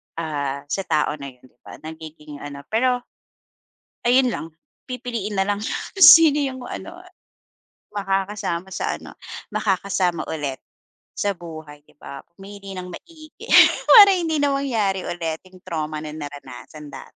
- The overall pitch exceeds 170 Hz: Yes, medium, 185 Hz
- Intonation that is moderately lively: No, wide, 8.0 semitones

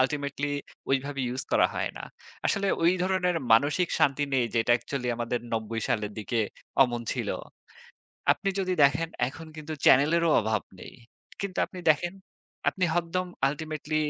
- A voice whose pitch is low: No, medium, 145 Hz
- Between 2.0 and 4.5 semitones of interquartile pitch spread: No, wide, 5.4 semitones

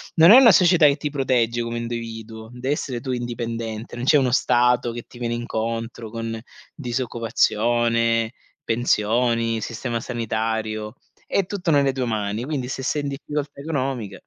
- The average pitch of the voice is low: Yes, low, 120 Hz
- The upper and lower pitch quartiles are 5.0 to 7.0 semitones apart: No, average, 2.7 semitones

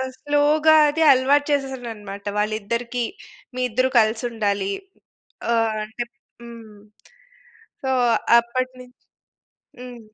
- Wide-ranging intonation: No, average, 3.0 semitones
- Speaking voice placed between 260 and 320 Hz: No, high, 240 Hz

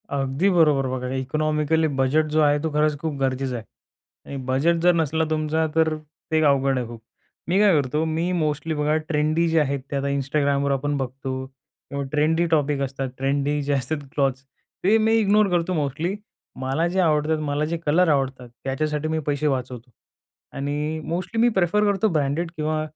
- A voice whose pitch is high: No, medium, 150 Hz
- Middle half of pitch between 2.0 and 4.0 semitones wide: Yes, average, 2.8 semitones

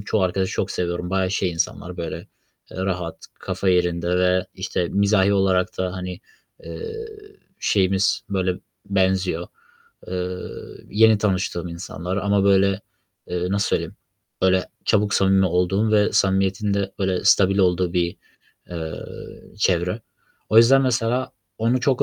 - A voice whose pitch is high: No, very low, 95 Hz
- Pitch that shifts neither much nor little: No, narrow, 2.0 semitones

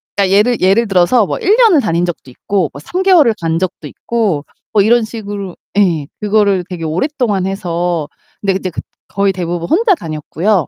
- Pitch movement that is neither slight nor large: Yes, average, 4.4 semitones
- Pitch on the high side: Yes, high, 195 Hz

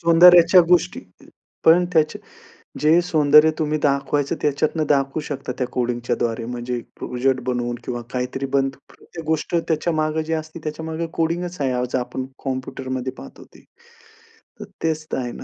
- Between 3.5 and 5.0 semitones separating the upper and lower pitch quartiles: Yes, average, 3.9 semitones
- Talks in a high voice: No, medium, 150 Hz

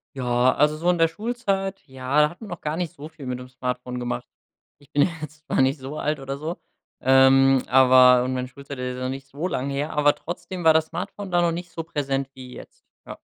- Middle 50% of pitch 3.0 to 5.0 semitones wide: Yes, average, 4.1 semitones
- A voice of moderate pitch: Yes, medium, 145 Hz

